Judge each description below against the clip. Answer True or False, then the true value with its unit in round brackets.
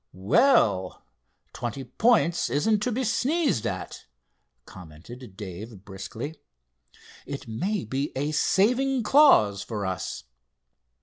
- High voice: False (135 Hz)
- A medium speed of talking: False (105 wpm)